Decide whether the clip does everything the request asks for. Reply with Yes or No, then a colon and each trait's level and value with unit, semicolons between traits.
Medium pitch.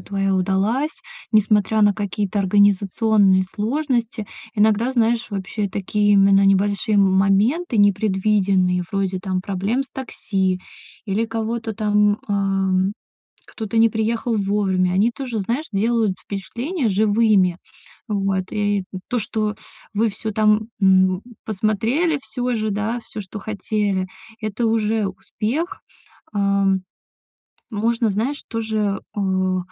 No: high, 210 Hz